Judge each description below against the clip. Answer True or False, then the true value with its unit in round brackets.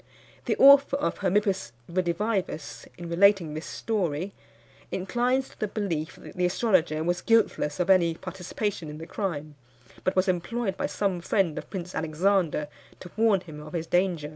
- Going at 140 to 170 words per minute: True (165 wpm)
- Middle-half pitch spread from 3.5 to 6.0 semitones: True (3.8 semitones)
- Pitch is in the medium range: True (180 Hz)